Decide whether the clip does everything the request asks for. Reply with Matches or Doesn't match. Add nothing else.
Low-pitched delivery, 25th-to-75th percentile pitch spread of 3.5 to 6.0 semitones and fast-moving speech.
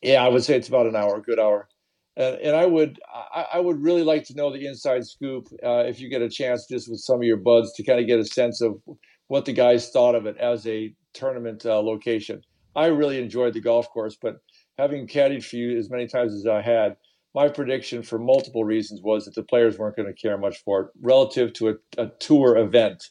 Doesn't match